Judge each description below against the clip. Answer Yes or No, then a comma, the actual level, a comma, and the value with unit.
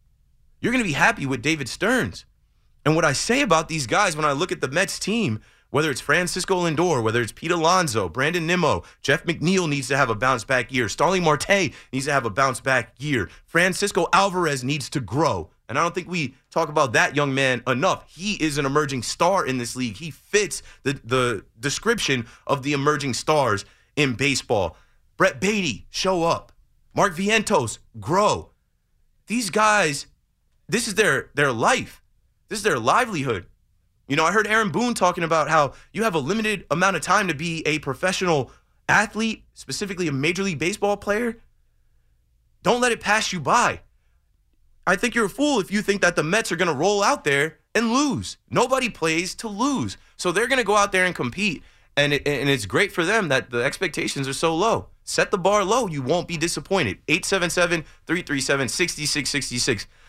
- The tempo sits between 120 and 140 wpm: No, average, 190 wpm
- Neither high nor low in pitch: Yes, medium, 160 Hz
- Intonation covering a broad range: Yes, wide, 6.3 semitones